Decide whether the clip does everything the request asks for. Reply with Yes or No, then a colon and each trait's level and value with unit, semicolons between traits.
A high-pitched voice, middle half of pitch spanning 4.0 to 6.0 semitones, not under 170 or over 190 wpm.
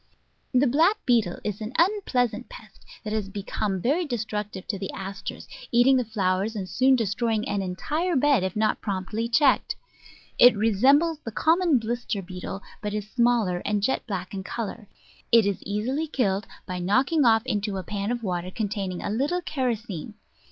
Yes: high, 220 Hz; average, 4.5 semitones; average, 175 wpm